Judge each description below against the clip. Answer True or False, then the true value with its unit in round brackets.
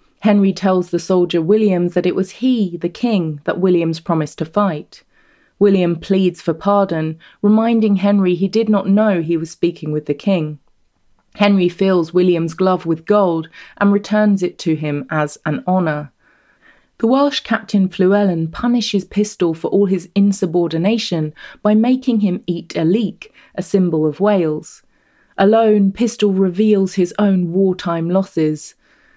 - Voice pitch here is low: False (185 Hz)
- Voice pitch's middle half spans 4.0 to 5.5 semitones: False (3.4 semitones)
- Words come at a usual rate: True (150 wpm)